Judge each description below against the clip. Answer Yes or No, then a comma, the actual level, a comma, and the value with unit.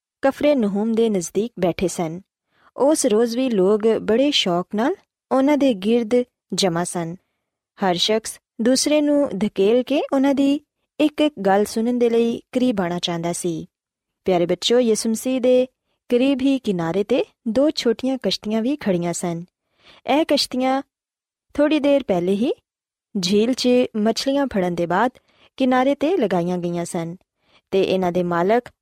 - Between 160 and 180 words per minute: No, average, 150 wpm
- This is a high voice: Yes, high, 225 Hz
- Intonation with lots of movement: Yes, wide, 6.1 semitones